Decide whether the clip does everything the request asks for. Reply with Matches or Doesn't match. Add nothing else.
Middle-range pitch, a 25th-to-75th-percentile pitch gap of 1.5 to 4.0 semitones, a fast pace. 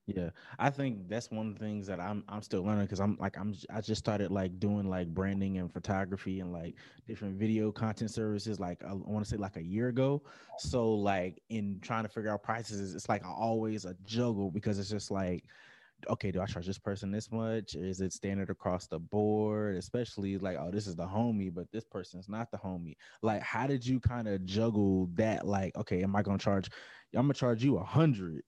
Doesn't match